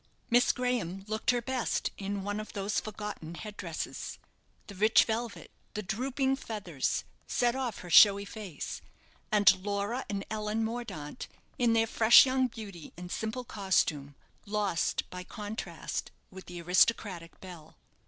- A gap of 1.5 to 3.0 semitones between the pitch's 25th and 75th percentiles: No, average, 3.5 semitones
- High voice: Yes, high, 210 Hz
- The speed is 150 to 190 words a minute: No, average, 140 wpm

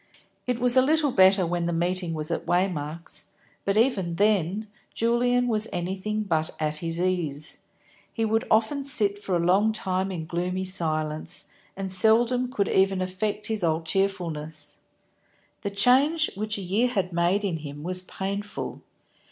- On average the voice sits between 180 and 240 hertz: Yes, high, 190 Hz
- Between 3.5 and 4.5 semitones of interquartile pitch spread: Yes, average, 4.1 semitones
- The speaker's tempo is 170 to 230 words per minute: No, average, 160 wpm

